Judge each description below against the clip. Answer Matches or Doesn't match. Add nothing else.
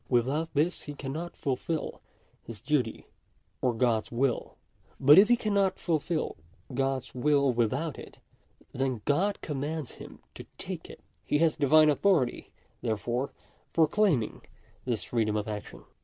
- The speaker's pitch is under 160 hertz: Matches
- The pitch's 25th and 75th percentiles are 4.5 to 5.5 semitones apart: Matches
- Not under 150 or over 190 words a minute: Doesn't match